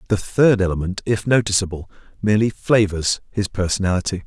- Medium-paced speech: No, slow, 125 wpm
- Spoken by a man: Yes, male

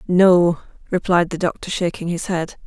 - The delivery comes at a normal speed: Yes, average, 155 wpm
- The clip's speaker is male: No, female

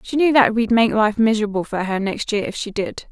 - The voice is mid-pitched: No, high, 220 Hz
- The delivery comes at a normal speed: No, fast, 270 wpm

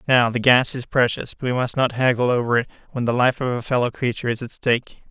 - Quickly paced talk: Yes, fast, 260 wpm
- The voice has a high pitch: No, low, 125 Hz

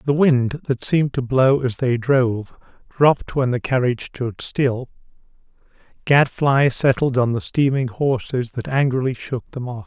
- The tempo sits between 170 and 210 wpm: No, average, 160 wpm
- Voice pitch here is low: Yes, low, 130 Hz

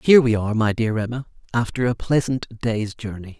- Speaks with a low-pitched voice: Yes, low, 115 Hz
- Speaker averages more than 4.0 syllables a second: Yes, 5.6 syllables/s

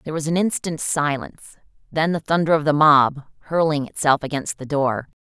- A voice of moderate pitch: Yes, medium, 150 Hz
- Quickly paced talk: No, average, 185 wpm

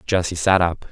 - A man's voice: Yes, male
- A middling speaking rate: Yes, average, 195 wpm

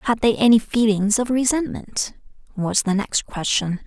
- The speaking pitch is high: Yes, high, 220 Hz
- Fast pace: No, average, 155 wpm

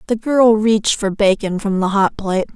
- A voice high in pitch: Yes, high, 210 Hz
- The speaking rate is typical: No, fast, 210 wpm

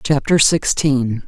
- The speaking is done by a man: No, female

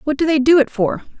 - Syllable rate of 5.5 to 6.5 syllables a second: Yes, 6.2 syllables/s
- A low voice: No, very high, 280 Hz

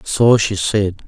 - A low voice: Yes, low, 100 Hz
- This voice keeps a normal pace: Yes, average, 170 wpm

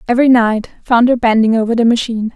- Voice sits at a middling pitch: No, high, 235 Hz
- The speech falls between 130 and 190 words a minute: No, fast, 205 wpm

